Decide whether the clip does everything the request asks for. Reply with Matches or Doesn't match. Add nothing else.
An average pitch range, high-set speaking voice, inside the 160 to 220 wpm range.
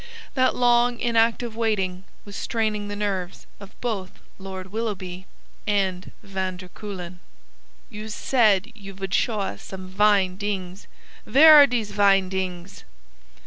Doesn't match